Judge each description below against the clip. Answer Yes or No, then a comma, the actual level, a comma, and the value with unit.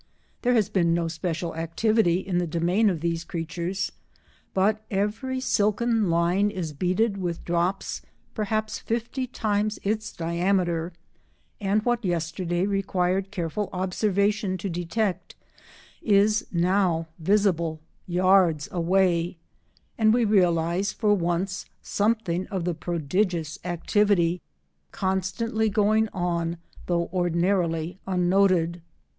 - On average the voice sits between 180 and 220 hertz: Yes, medium, 185 Hz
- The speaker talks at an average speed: No, slow, 110 wpm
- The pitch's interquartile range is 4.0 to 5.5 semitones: No, average, 3.3 semitones